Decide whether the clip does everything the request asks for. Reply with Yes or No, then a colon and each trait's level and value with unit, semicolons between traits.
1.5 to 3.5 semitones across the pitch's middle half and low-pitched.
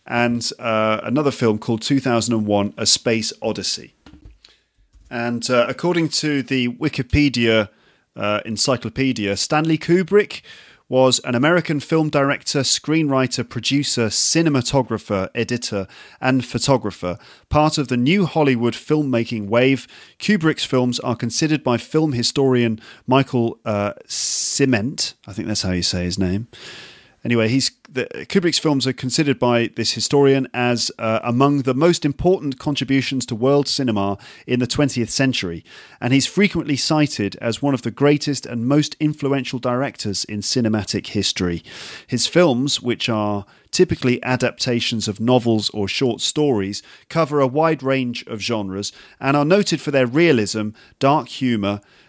No: average, 4.1 semitones; low, 125 Hz